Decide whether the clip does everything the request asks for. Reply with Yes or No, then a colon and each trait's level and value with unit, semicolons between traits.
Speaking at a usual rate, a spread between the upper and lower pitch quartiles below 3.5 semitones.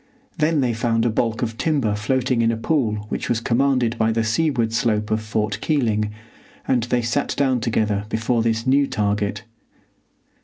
Yes: average, 170 wpm; average, 2.8 semitones